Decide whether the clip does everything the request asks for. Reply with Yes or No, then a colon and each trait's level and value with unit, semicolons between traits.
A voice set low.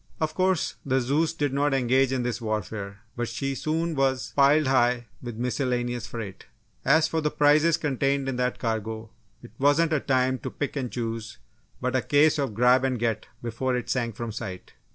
Yes: low, 130 Hz